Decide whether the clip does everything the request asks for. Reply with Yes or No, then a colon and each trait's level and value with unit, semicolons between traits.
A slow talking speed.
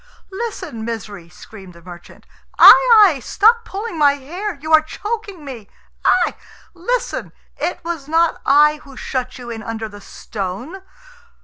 No: average, 145 wpm